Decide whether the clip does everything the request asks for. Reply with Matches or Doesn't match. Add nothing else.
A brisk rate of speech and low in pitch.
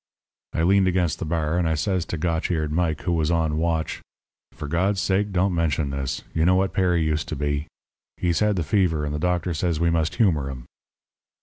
Matches